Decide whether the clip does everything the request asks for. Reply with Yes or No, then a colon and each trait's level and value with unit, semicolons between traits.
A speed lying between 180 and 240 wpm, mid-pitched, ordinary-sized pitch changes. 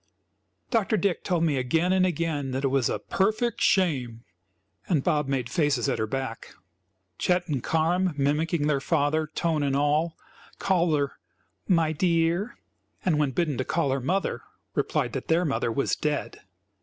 No: average, 165 wpm; medium, 155 Hz; average, 4.1 semitones